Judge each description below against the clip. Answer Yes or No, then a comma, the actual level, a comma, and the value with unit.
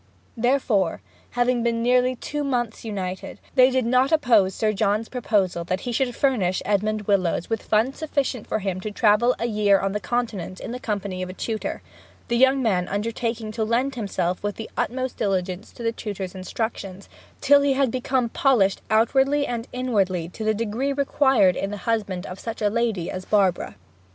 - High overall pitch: Yes, high, 220 Hz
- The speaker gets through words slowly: No, average, 180 wpm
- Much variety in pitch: No, average, 4.2 semitones